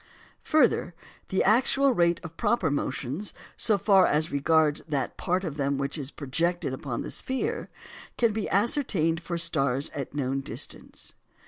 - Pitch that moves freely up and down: Yes, wide, 5.9 semitones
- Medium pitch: Yes, medium, 165 Hz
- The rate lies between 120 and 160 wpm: Yes, average, 150 wpm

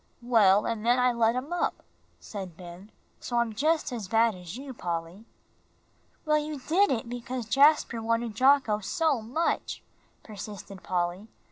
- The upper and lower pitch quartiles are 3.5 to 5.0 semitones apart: Yes, average, 4.4 semitones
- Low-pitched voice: No, high, 230 Hz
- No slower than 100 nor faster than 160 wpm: Yes, average, 150 wpm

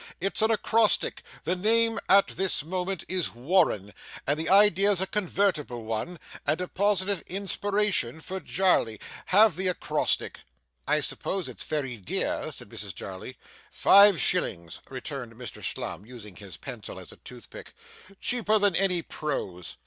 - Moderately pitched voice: Yes, medium, 180 Hz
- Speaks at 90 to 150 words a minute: Yes, average, 145 wpm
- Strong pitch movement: Yes, wide, 8.0 semitones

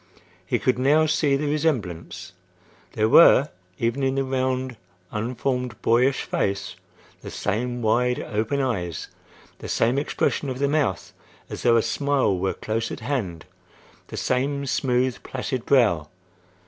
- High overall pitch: No, low, 125 Hz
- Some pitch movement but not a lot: Yes, average, 3.8 semitones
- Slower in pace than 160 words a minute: Yes, average, 140 wpm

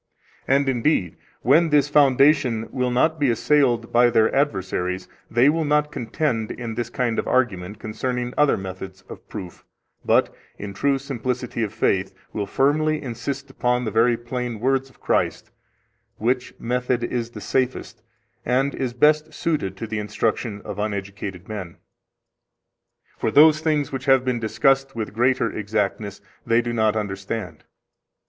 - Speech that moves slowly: No, average, 150 wpm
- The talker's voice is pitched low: Yes, low, 120 Hz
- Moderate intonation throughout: Yes, average, 3.9 semitones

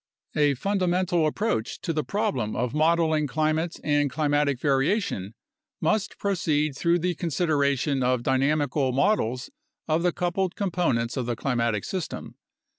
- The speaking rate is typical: No, slow, 130 wpm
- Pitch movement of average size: Yes, average, 4.7 semitones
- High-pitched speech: No, medium, 150 Hz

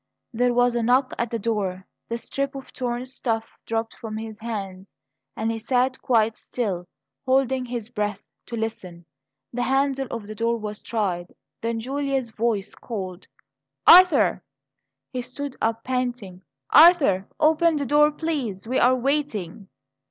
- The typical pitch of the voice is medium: No, high, 235 Hz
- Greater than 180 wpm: No, average, 150 wpm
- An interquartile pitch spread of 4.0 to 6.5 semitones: No, average, 3.4 semitones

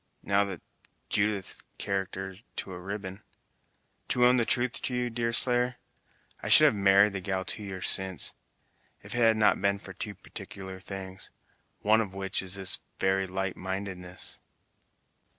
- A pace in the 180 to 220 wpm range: No, average, 150 wpm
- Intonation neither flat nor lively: No, narrow, 2.1 semitones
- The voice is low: Yes, low, 100 Hz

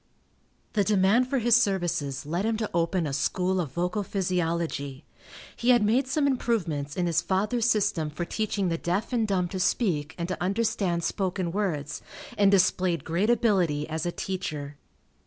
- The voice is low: No, medium, 185 Hz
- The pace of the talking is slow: No, average, 170 wpm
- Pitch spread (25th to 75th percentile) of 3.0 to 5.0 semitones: Yes, average, 4.3 semitones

